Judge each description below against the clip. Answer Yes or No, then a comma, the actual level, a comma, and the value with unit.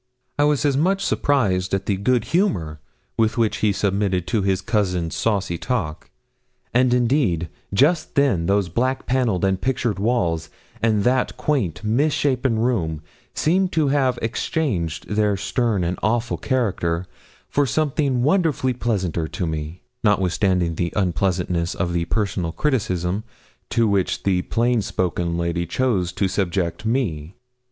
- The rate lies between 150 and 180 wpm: No, average, 140 wpm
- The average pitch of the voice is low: Yes, low, 105 Hz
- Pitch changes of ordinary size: No, wide, 6.2 semitones